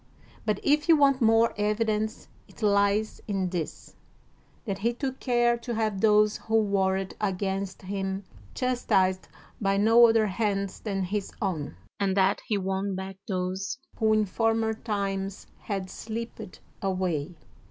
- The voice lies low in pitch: No, high, 205 Hz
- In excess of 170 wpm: No, average, 140 wpm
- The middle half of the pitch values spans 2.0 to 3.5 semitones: Yes, narrow, 2.6 semitones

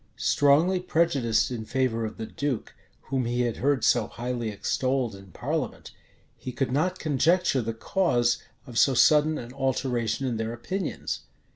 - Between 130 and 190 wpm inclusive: Yes, average, 155 wpm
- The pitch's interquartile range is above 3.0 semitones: Yes, average, 3.7 semitones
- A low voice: Yes, low, 125 Hz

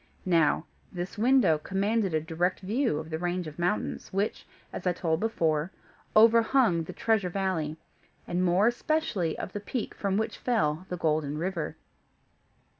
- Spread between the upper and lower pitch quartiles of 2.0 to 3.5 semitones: No, average, 4.8 semitones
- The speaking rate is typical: Yes, average, 155 wpm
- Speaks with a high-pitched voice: No, medium, 180 Hz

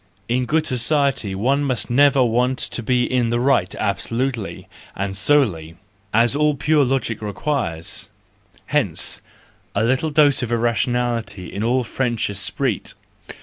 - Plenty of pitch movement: No, average, 4.0 semitones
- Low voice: Yes, low, 120 Hz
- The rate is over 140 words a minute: No, slow, 135 wpm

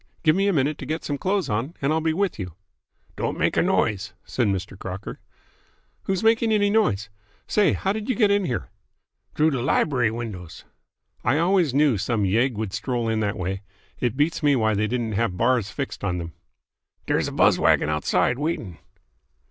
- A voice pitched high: No, low, 125 Hz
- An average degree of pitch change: No, wide, 7.6 semitones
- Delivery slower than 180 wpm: No, average, 195 wpm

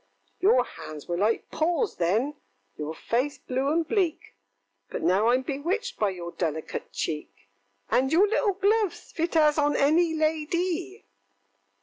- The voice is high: Yes, very high, 295 Hz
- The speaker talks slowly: No, average, 145 wpm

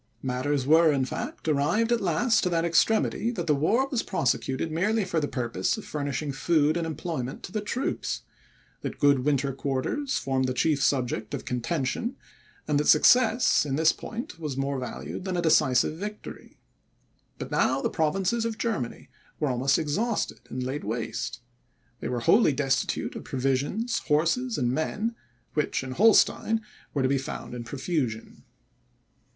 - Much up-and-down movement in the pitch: Yes, wide, 7.1 semitones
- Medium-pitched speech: Yes, medium, 150 Hz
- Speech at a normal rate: Yes, average, 165 wpm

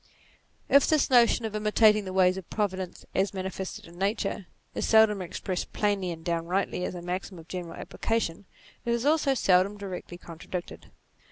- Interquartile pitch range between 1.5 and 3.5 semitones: Yes, average, 2.9 semitones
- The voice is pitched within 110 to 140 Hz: No, high, 190 Hz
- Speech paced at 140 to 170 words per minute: Yes, average, 165 wpm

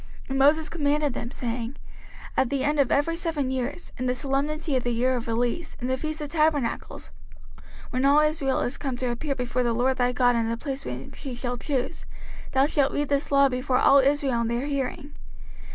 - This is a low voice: No, very high, 270 Hz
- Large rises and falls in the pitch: No, average, 2.8 semitones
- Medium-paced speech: No, fast, 215 wpm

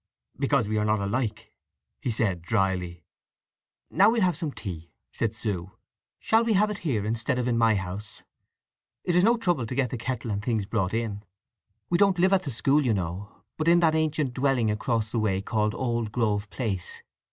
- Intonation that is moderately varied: No, wide, 5.9 semitones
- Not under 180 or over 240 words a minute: Yes, average, 195 wpm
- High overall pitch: No, low, 115 Hz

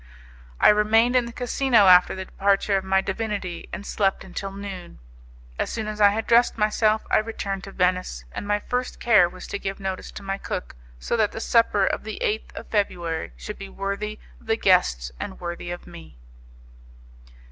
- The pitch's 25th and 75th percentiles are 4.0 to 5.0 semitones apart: No, narrow, 2.5 semitones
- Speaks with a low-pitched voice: No, high, 200 Hz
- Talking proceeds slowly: No, average, 190 wpm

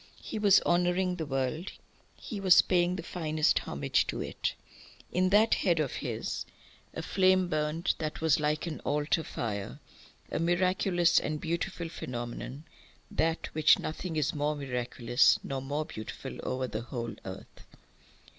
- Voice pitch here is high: No, medium, 155 Hz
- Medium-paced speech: Yes, average, 145 wpm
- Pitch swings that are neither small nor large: Yes, average, 4.6 semitones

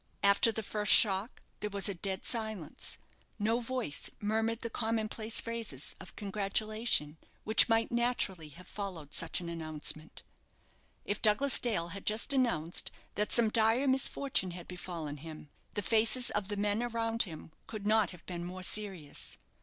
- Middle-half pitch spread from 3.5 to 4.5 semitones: Yes, average, 4.1 semitones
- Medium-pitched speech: No, high, 210 Hz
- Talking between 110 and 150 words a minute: No, average, 160 wpm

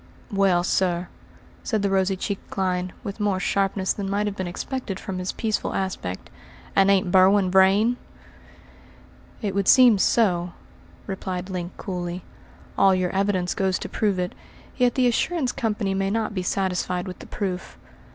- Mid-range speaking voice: No, high, 195 Hz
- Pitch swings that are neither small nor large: No, narrow, 1.9 semitones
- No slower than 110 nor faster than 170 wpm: Yes, average, 160 wpm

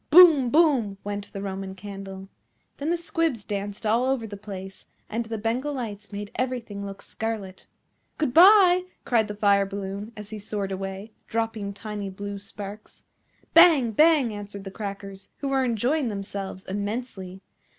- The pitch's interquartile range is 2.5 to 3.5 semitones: No, average, 3.9 semitones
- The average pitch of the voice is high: Yes, high, 210 Hz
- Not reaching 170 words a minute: Yes, average, 155 wpm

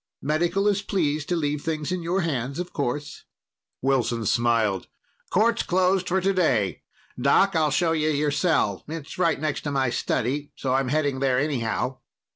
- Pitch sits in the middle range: Yes, medium, 150 Hz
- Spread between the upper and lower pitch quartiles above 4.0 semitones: Yes, average, 4.6 semitones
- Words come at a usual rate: Yes, average, 165 wpm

